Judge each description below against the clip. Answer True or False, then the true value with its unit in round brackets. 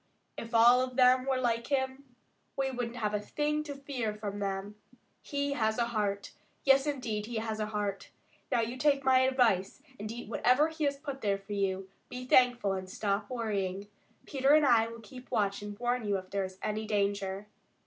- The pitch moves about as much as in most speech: True (4.1 semitones)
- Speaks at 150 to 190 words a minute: False (200 wpm)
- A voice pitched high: True (230 Hz)